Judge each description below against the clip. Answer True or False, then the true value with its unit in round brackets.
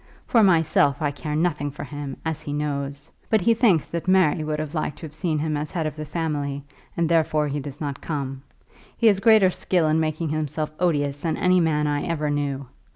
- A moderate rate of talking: False (220 wpm)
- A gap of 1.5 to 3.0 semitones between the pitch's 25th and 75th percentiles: True (2.5 semitones)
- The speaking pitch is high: False (155 Hz)